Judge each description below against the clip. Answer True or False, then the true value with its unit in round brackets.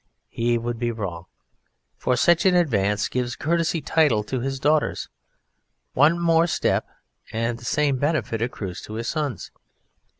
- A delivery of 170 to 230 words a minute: False (155 wpm)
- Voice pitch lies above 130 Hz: False (125 Hz)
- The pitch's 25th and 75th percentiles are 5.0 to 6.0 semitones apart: True (5.3 semitones)